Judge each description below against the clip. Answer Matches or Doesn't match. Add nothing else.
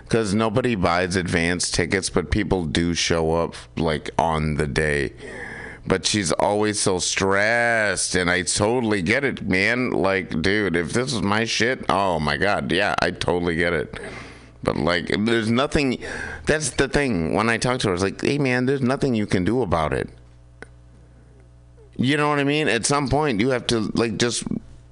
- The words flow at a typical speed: Matches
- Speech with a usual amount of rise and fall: Doesn't match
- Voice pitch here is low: Matches